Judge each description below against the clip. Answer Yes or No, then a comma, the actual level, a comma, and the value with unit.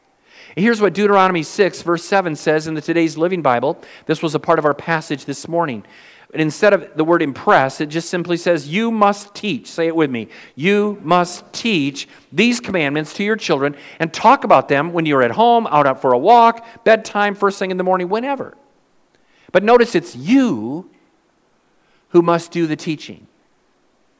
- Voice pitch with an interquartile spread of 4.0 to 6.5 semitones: Yes, average, 4.7 semitones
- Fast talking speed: No, average, 185 wpm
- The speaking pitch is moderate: Yes, medium, 170 Hz